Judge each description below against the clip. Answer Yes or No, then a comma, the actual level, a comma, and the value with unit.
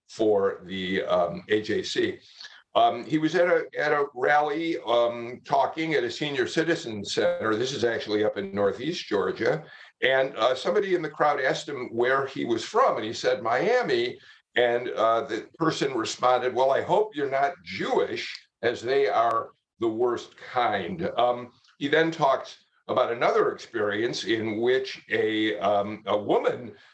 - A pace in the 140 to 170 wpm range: Yes, average, 160 wpm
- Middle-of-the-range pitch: Yes, medium, 145 Hz